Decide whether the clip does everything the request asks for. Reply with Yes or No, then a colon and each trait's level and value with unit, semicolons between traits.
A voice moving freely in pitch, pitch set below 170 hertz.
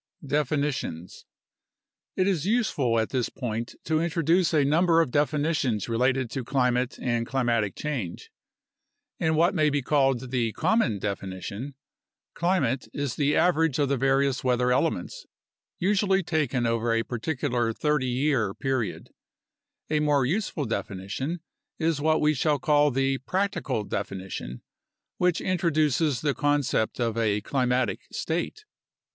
No: average, 4.7 semitones; low, 135 Hz